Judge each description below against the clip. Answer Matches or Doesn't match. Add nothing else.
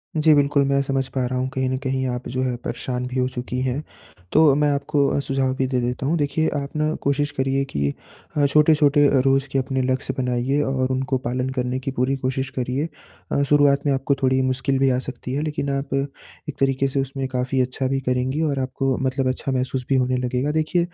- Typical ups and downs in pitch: Doesn't match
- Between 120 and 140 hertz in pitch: Matches